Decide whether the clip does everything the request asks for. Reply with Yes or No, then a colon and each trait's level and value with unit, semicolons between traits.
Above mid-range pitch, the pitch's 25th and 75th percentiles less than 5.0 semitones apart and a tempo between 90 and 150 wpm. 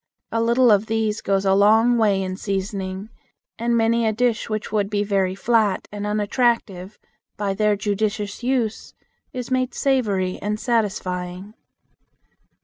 Yes: high, 210 Hz; average, 2.7 semitones; average, 140 wpm